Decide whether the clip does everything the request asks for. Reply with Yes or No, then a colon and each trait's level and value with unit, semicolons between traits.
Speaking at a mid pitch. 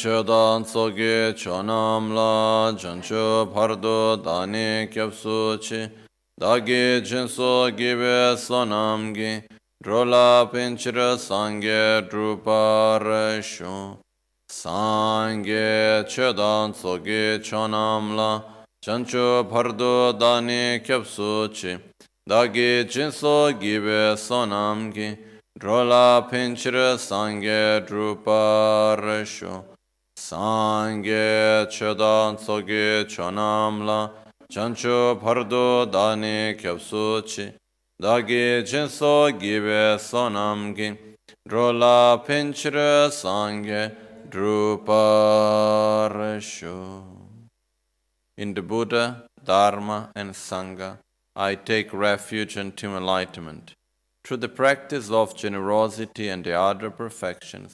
No: low, 110 Hz